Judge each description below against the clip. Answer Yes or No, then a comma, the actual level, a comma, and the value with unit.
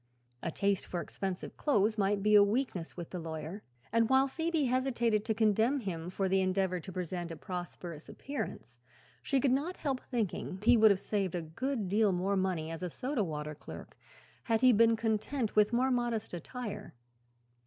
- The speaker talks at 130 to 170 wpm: No, average, 180 wpm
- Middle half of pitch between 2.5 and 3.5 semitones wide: No, average, 5.0 semitones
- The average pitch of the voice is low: No, high, 205 Hz